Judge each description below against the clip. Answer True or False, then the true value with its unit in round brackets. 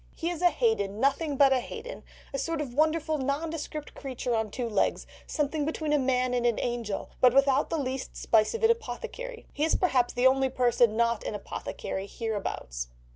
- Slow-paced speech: False (190 wpm)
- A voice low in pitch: False (265 Hz)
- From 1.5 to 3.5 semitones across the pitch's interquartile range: False (4.6 semitones)